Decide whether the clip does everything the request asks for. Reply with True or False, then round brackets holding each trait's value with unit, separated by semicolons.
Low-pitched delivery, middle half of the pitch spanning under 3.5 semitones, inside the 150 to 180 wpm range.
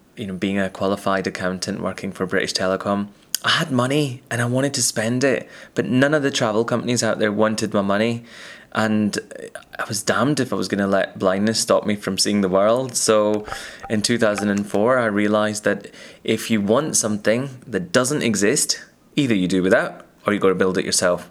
False (105 Hz; 2.9 semitones; 205 wpm)